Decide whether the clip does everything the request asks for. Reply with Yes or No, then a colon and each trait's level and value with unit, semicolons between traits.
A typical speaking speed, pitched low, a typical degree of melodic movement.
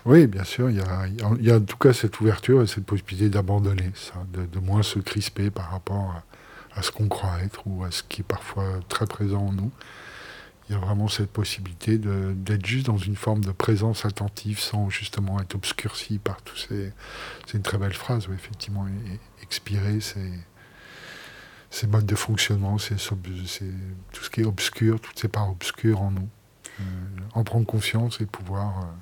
No: average, 200 wpm; low, 100 Hz; narrow, 2.1 semitones